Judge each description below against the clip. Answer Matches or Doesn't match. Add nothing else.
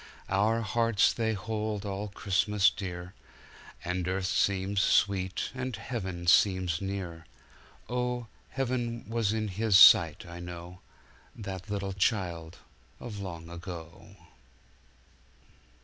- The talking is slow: Matches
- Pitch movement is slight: Doesn't match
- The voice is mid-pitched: Doesn't match